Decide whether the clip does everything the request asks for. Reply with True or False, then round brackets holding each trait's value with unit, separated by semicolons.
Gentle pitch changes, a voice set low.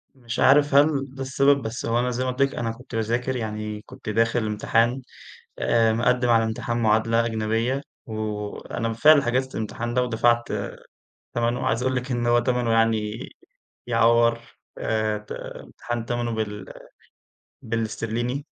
True (2.0 semitones; 115 Hz)